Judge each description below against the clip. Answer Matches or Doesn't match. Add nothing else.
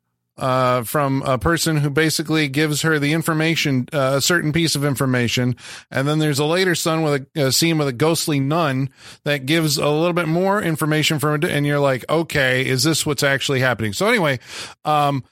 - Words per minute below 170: Doesn't match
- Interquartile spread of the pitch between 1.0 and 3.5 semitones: Matches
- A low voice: Doesn't match